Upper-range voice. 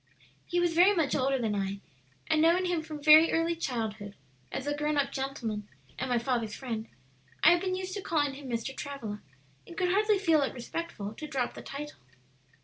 Yes: very high, 285 Hz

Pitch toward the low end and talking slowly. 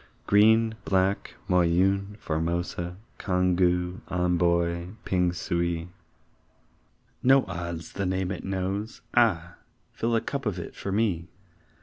Yes: very low, 90 Hz; slow, 105 wpm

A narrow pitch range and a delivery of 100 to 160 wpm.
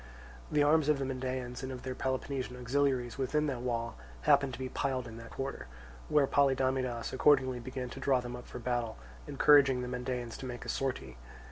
No: narrow, 1.7 semitones; average, 195 wpm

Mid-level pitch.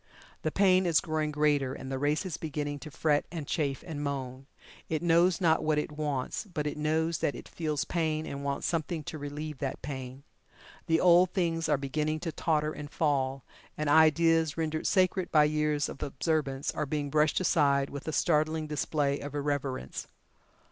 Yes: medium, 150 Hz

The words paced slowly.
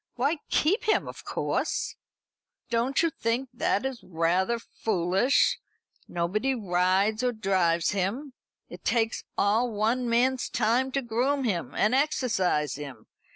Yes: slow, 130 wpm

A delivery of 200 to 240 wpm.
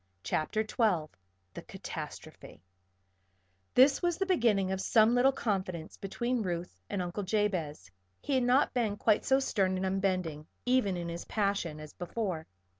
No: average, 150 wpm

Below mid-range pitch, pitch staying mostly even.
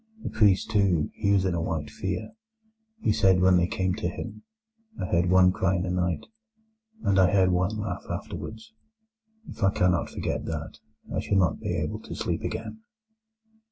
Yes: very low, 95 Hz; narrow, 2.1 semitones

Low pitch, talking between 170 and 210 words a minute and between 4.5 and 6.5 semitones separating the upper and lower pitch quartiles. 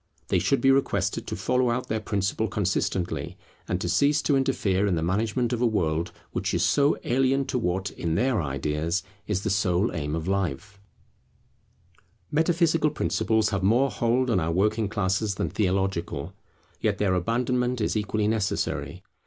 Yes: low, 105 Hz; average, 175 wpm; average, 5.2 semitones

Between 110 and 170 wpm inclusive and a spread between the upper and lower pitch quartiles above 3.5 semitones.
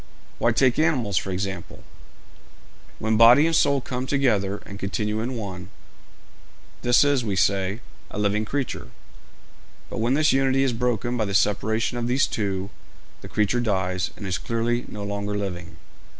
Yes: average, 160 wpm; average, 4.0 semitones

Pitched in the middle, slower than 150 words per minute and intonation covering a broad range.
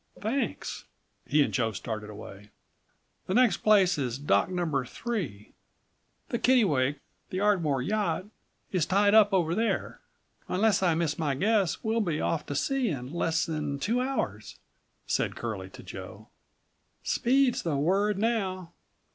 Yes: medium, 180 Hz; average, 140 wpm; wide, 6.8 semitones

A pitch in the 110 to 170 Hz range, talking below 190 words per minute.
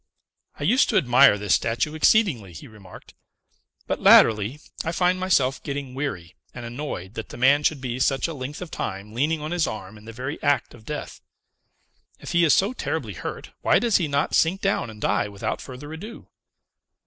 No: medium, 140 Hz; average, 195 wpm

